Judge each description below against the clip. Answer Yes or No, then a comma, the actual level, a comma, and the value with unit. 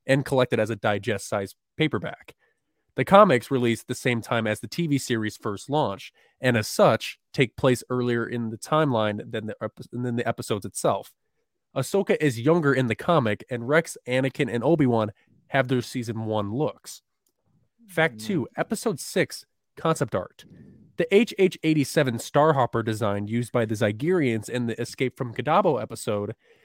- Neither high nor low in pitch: No, low, 125 Hz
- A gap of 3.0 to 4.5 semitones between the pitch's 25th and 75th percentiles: No, average, 5.2 semitones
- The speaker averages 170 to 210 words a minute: No, average, 160 wpm